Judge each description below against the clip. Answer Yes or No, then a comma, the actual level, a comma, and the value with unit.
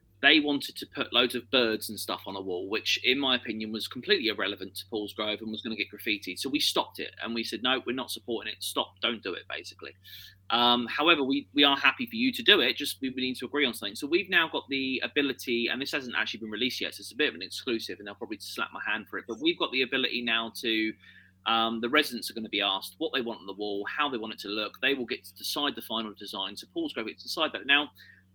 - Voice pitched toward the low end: Yes, low, 115 Hz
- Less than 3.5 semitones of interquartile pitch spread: No, average, 4.8 semitones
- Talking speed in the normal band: No, fast, 280 wpm